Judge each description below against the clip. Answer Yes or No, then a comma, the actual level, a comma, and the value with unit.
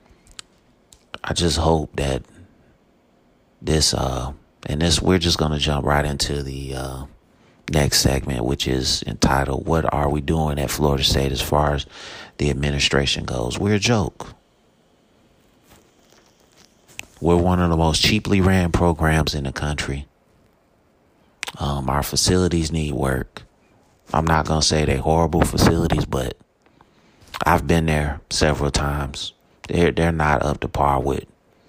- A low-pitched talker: Yes, very low, 75 Hz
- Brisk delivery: No, average, 140 wpm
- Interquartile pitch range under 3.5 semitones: Yes, average, 2.8 semitones